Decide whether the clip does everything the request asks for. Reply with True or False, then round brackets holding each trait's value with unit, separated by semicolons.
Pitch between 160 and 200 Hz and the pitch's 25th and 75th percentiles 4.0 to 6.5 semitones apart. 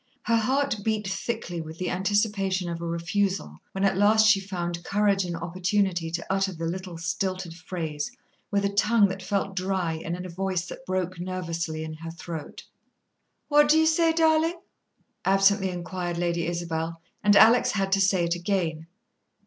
False (185 Hz; 3.1 semitones)